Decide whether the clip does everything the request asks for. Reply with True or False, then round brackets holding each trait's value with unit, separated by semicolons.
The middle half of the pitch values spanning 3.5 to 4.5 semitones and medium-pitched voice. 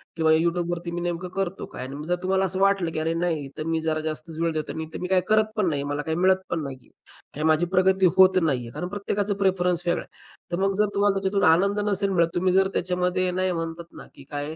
False (2.9 semitones; 175 Hz)